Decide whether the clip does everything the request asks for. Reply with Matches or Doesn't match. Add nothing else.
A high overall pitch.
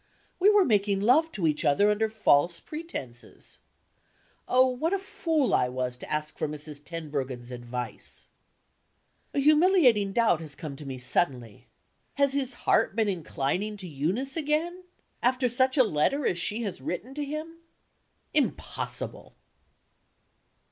Matches